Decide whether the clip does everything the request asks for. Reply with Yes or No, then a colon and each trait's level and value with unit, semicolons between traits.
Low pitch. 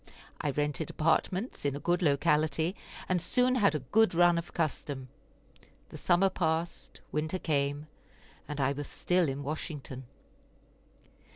No: medium, 155 Hz